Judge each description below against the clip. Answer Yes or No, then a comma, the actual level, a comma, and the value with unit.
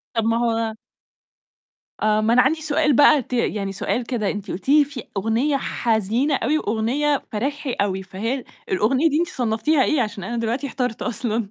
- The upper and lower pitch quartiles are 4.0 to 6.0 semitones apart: Yes, average, 4.4 semitones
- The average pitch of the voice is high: Yes, high, 235 Hz